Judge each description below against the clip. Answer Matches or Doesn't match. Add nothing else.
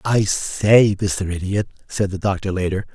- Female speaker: Doesn't match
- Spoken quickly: Doesn't match